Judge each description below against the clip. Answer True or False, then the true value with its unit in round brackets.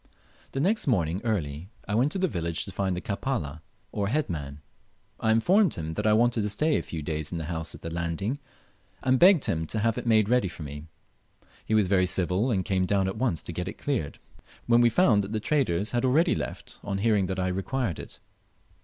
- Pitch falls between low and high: False (100 Hz)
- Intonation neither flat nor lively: False (6.0 semitones)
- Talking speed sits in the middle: False (225 wpm)